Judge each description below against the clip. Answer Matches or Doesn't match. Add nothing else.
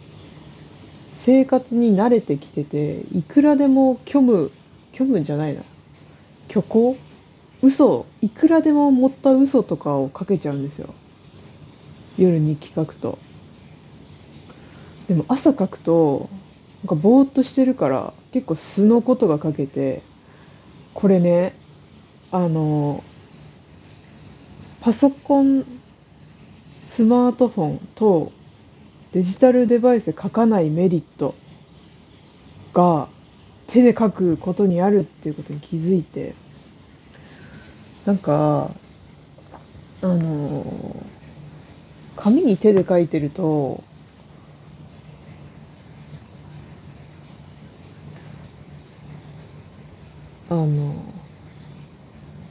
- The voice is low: Doesn't match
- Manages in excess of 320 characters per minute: Doesn't match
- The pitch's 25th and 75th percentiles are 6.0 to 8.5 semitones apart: Matches